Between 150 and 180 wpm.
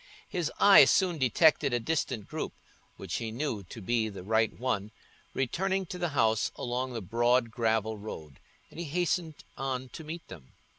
Yes: average, 170 wpm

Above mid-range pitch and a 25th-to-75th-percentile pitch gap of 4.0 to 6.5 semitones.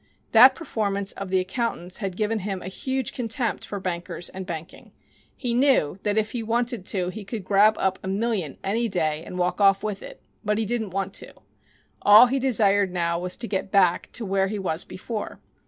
No: high, 200 Hz; average, 3.3 semitones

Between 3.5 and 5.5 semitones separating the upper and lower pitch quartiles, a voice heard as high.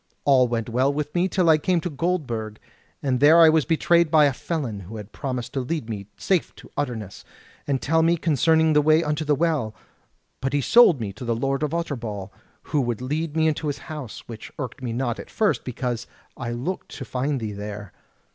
No: average, 5.1 semitones; medium, 140 Hz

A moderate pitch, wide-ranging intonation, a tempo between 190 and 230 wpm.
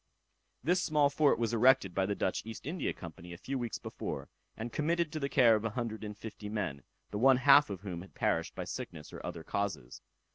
No: low, 115 Hz; wide, 5.9 semitones; fast, 205 wpm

